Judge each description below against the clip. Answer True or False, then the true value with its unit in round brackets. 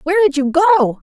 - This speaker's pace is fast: True (215 wpm)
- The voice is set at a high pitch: True (320 Hz)